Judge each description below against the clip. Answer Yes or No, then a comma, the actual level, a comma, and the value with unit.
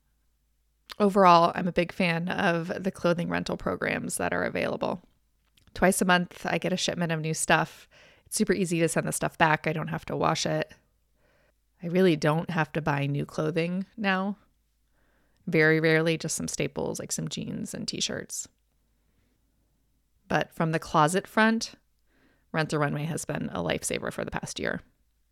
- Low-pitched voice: No, medium, 165 Hz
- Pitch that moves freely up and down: No, average, 3.1 semitones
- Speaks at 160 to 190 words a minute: Yes, average, 170 wpm